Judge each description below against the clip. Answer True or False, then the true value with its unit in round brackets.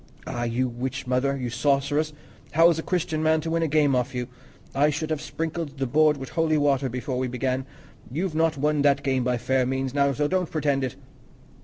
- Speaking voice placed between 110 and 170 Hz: True (140 Hz)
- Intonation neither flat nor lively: True (3.2 semitones)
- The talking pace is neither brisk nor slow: False (215 wpm)